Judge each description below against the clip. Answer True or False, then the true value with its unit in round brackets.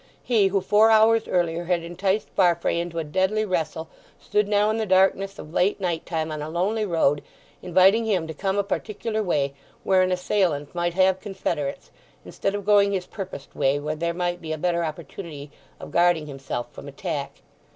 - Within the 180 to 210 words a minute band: True (190 wpm)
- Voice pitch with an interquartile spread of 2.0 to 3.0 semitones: False (3.6 semitones)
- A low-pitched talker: False (180 Hz)